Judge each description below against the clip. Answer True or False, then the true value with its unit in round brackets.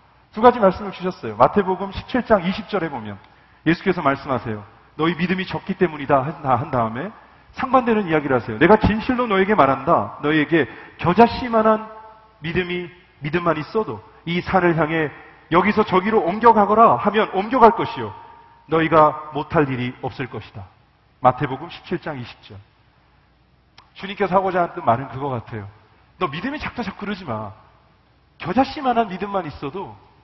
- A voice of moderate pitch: True (170 Hz)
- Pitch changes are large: True (7.1 semitones)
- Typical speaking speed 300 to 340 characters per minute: True (325 characters per minute)